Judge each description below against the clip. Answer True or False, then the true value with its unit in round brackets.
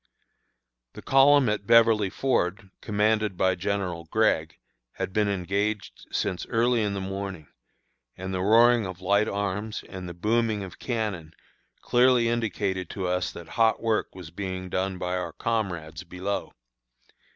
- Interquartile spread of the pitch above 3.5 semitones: False (3.2 semitones)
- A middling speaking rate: True (145 wpm)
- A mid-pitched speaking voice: False (100 Hz)